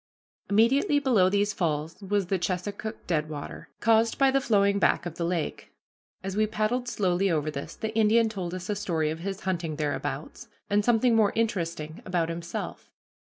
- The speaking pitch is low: No, high, 195 Hz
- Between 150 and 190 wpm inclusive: Yes, average, 170 wpm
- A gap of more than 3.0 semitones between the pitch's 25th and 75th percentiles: Yes, average, 4.4 semitones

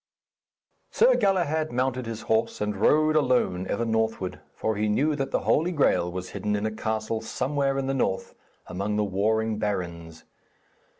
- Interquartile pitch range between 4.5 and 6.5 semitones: Yes, average, 4.9 semitones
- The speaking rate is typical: Yes, average, 165 wpm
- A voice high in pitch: No, low, 110 Hz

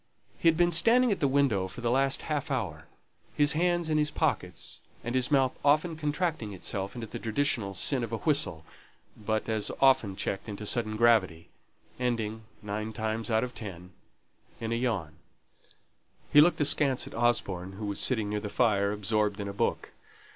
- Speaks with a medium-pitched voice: No, low, 115 Hz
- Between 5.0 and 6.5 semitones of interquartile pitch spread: Yes, wide, 5.6 semitones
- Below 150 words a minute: No, average, 180 wpm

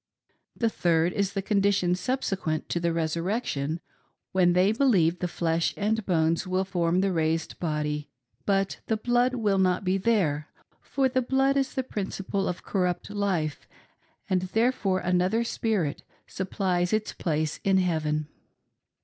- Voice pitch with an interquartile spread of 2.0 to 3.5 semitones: No, average, 4.0 semitones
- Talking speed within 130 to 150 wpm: Yes, average, 145 wpm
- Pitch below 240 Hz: Yes, medium, 185 Hz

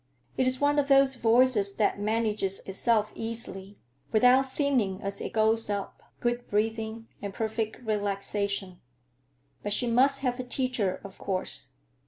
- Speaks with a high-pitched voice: Yes, high, 220 Hz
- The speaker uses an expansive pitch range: No, average, 3.6 semitones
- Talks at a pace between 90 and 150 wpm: Yes, average, 145 wpm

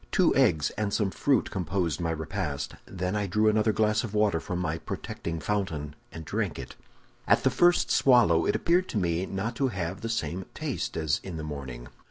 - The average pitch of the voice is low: Yes, very low, 95 Hz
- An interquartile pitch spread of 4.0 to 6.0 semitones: Yes, average, 4.8 semitones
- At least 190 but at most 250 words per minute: Yes, average, 200 wpm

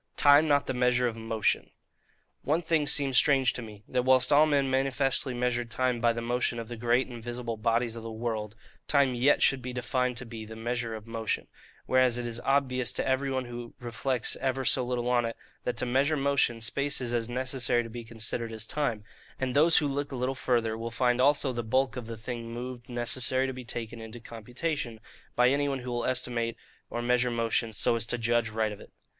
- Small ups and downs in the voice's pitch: Yes, narrow, 2.2 semitones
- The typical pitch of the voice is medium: No, low, 125 Hz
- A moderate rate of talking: No, fast, 220 wpm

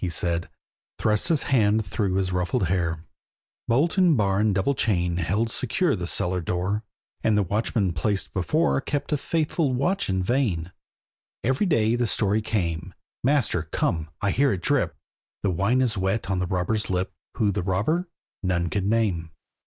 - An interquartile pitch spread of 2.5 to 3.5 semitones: No, average, 5.1 semitones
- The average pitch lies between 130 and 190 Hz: No, low, 100 Hz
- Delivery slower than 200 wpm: Yes, average, 170 wpm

